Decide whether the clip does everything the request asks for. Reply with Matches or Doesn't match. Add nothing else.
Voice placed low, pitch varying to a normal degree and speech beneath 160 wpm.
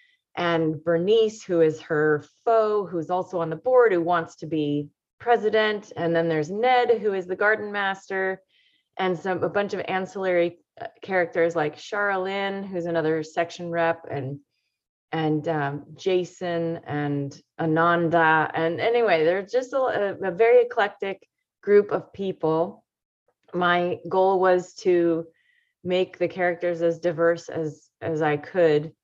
Doesn't match